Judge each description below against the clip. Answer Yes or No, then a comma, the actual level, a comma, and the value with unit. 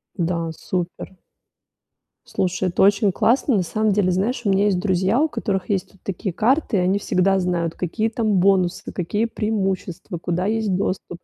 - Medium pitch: No, high, 195 Hz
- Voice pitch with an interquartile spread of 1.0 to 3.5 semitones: Yes, average, 2.8 semitones